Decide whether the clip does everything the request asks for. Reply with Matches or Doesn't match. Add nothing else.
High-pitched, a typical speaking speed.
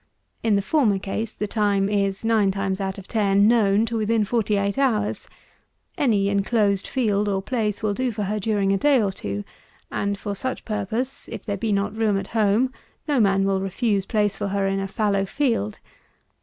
Matches